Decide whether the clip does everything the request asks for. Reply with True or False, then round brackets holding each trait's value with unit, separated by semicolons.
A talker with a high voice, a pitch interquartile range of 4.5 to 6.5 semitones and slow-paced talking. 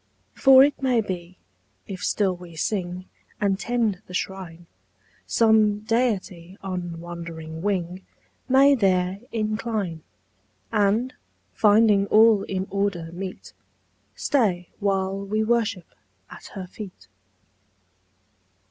False (195 Hz; 3.3 semitones; 105 wpm)